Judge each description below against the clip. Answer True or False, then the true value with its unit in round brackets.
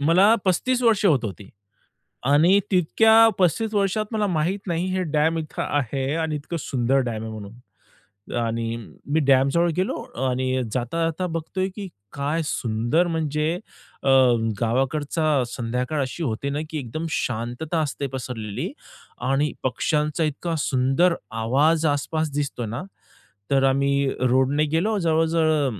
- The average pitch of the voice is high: False (150 Hz)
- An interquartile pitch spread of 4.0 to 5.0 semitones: True (4.3 semitones)